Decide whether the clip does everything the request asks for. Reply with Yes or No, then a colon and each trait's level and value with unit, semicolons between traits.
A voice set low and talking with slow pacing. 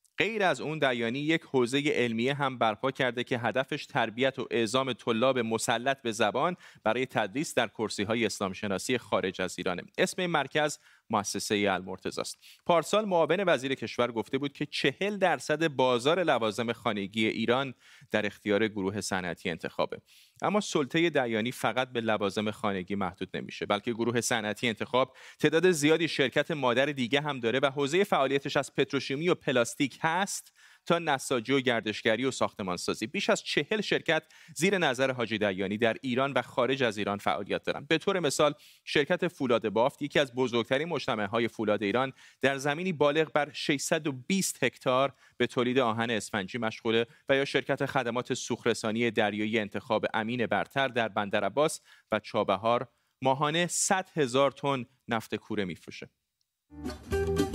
No: low, 130 Hz; fast, 155 wpm